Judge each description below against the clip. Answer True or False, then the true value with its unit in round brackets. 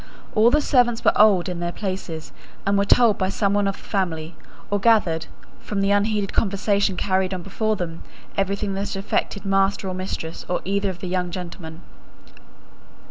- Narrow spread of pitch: True (2.1 semitones)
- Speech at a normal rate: True (180 wpm)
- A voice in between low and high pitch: False (195 Hz)